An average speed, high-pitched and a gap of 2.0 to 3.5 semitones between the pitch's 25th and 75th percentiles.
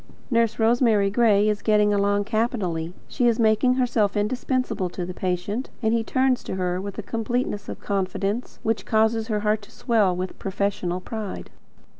Yes: average, 170 wpm; high, 210 Hz; average, 2.7 semitones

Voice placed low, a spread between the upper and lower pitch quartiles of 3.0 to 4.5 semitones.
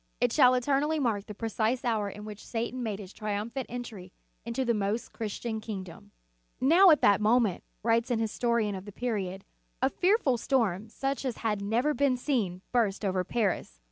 No: high, 225 Hz; average, 3.5 semitones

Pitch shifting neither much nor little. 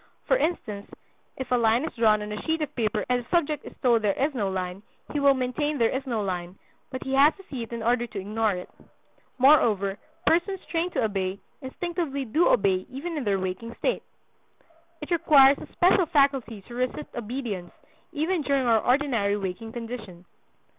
No: wide, 5.7 semitones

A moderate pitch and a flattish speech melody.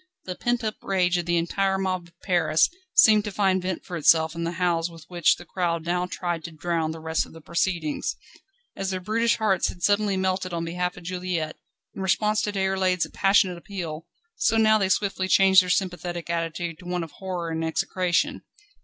Yes: medium, 180 Hz; narrow, 2.3 semitones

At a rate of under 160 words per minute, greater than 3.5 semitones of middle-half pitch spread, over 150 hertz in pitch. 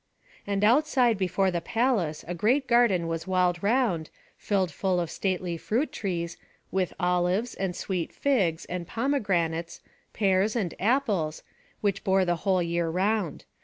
Yes: average, 145 wpm; average, 4.0 semitones; high, 190 Hz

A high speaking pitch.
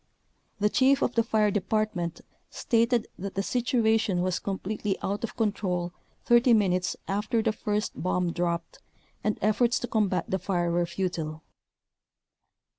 Yes: high, 205 Hz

